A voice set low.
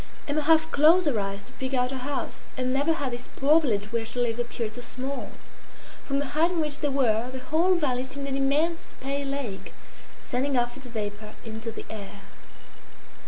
No: very high, 265 Hz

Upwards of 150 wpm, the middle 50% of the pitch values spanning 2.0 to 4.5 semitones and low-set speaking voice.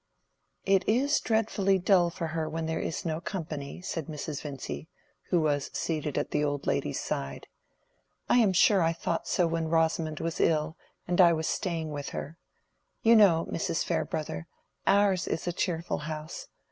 No: average, 170 wpm; average, 2.9 semitones; medium, 165 Hz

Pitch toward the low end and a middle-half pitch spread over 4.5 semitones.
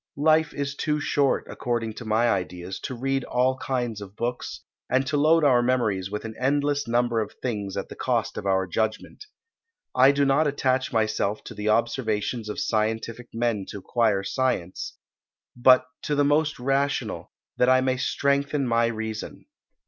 No: low, 120 Hz; average, 3.9 semitones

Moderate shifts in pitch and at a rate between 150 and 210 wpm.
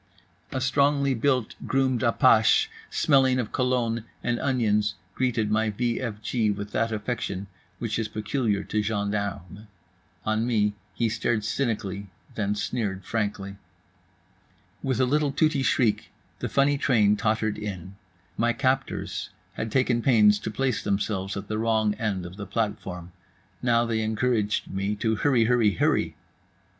No: average, 3.2 semitones; average, 140 wpm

